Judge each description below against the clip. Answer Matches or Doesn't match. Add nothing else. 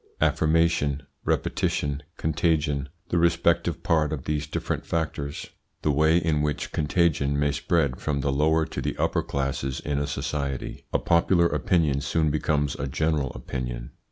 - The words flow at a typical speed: Matches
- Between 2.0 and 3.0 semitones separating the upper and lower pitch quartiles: Matches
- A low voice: Matches